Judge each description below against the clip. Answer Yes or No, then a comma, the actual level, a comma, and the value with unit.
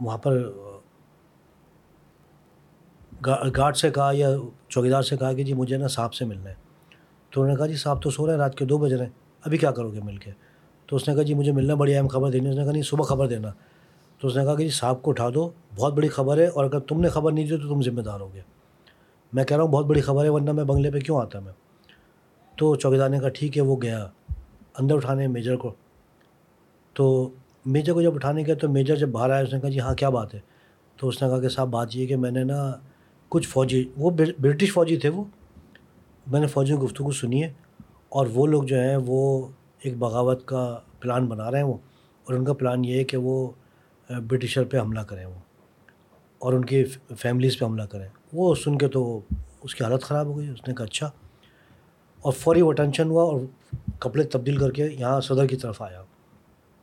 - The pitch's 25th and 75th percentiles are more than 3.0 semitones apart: No, average, 2.7 semitones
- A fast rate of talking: Yes, fast, 230 wpm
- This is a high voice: No, low, 135 Hz